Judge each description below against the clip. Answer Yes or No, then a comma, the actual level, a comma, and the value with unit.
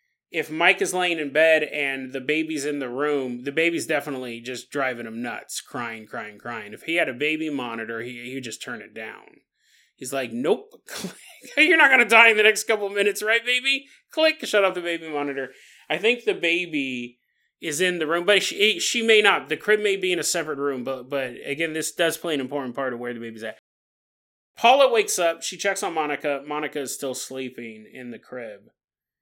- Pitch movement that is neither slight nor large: No, wide, 7.2 semitones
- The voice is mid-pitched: Yes, medium, 155 Hz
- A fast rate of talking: Yes, fast, 220 wpm